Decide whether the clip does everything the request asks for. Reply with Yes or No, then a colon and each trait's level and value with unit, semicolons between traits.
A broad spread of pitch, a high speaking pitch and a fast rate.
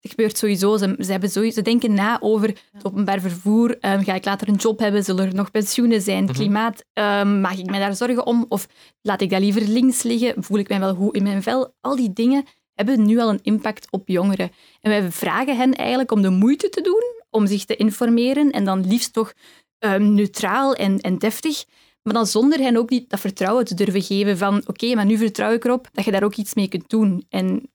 No: average, 3.0 semitones; high, 215 Hz; fast, 235 wpm